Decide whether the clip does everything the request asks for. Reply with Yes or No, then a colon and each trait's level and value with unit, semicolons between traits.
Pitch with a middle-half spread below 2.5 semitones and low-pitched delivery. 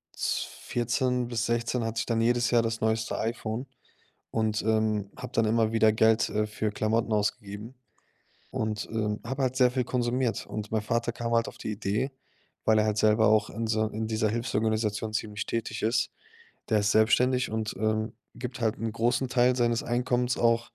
Yes: narrow, 1.6 semitones; low, 115 Hz